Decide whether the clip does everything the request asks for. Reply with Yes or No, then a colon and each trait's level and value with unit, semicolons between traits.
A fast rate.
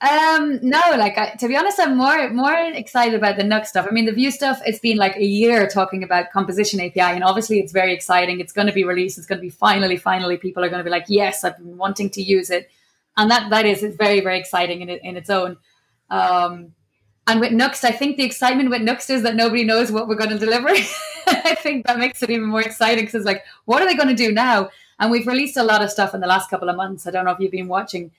Yes: fast, 270 wpm